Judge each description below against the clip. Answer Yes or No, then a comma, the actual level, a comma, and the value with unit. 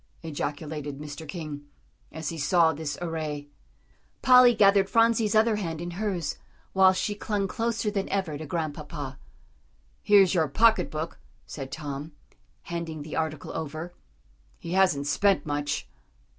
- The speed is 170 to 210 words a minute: No, slow, 135 wpm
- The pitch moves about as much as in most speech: Yes, average, 5.0 semitones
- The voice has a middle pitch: Yes, medium, 165 Hz